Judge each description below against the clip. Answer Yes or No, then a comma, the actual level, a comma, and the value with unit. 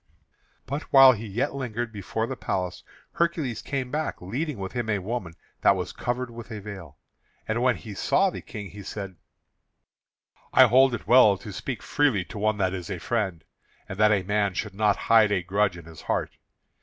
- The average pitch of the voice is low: Yes, low, 110 Hz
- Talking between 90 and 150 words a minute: No, average, 195 wpm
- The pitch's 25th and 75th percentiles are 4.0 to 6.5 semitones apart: Yes, average, 4.3 semitones